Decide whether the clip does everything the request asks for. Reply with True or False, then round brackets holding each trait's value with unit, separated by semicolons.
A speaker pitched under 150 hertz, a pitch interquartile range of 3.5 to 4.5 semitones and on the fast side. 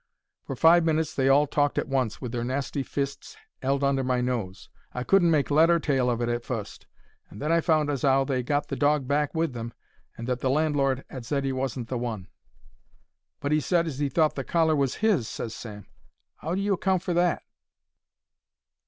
True (140 Hz; 3.8 semitones; 215 wpm)